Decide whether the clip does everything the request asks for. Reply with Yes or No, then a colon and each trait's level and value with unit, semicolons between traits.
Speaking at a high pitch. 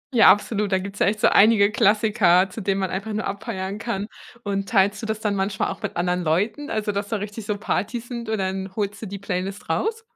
Yes: high, 205 Hz